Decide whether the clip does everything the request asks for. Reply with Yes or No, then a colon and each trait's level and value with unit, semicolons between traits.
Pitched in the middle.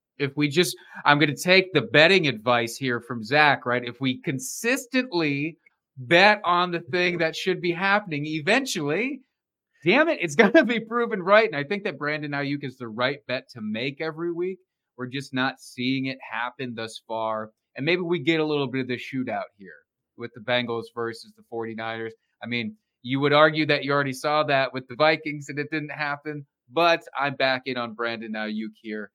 Yes: medium, 145 Hz